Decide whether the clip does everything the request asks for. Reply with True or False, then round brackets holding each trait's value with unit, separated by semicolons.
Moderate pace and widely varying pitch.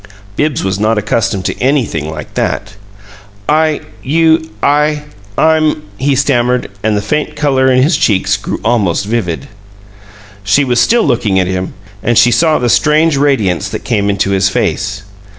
True (165 wpm; 6.7 semitones)